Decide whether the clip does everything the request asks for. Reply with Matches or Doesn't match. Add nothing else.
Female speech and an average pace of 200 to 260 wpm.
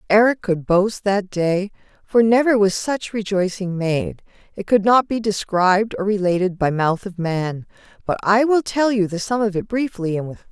Matches